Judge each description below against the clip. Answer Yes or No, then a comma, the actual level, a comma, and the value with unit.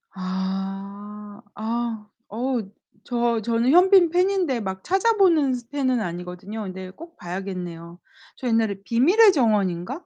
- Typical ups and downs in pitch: No, wide, 6.0 semitones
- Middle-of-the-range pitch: No, high, 225 Hz